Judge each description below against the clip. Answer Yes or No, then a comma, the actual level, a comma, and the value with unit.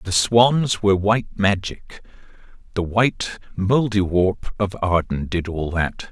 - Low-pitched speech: Yes, low, 100 Hz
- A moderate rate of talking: No, slow, 120 wpm